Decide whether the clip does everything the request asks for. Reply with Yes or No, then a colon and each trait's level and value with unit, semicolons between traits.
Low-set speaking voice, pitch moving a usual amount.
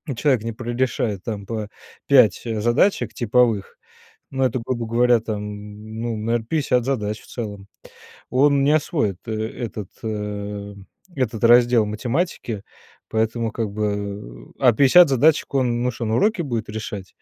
Yes: low, 115 Hz; average, 3.1 semitones